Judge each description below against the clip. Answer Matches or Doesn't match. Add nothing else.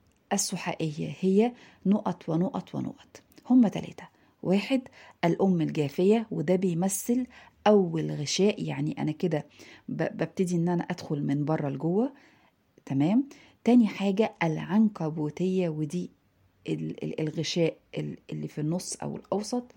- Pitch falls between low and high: Matches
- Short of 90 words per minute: Doesn't match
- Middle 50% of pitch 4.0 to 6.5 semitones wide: Matches